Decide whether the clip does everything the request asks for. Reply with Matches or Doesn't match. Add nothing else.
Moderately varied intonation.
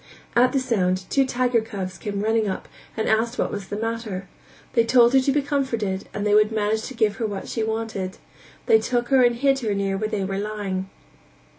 Matches